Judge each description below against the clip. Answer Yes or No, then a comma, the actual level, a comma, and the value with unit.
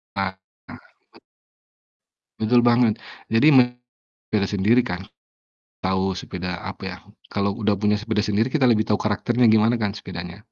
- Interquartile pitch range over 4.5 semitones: No, average, 2.9 semitones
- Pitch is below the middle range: Yes, low, 105 Hz